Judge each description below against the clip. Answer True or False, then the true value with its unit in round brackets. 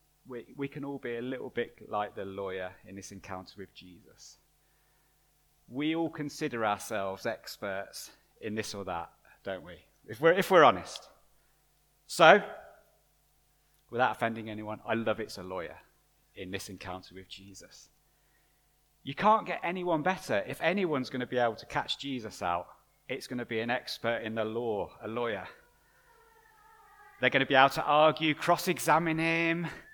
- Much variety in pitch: True (7.5 semitones)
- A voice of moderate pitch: False (125 Hz)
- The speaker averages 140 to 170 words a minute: True (165 wpm)